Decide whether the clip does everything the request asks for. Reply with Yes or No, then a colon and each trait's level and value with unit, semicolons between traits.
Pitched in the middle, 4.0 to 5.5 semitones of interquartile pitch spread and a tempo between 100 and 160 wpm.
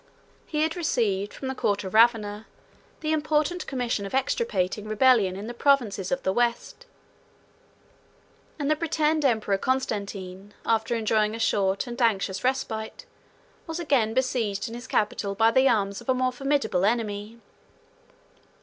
No: high, 230 Hz; average, 4.4 semitones; average, 150 wpm